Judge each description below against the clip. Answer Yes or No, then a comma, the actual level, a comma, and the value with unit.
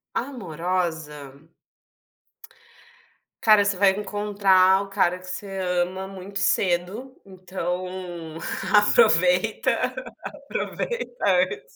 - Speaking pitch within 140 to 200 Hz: Yes, high, 190 Hz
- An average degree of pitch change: No, narrow, 2.3 semitones